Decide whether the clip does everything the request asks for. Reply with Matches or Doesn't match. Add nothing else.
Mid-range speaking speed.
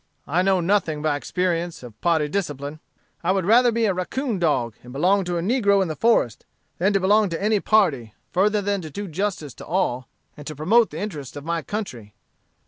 Doesn't match